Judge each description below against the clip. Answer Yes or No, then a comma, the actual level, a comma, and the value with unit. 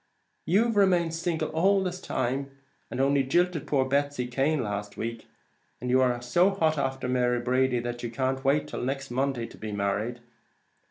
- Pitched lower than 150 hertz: Yes, low, 135 Hz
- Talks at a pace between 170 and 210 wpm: Yes, average, 175 wpm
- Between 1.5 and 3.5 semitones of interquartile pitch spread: No, average, 4.4 semitones